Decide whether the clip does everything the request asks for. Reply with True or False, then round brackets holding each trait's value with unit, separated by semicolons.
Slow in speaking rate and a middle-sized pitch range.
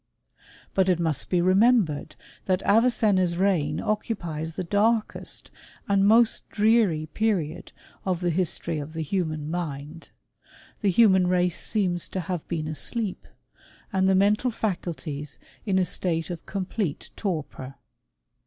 True (130 wpm; 3.9 semitones)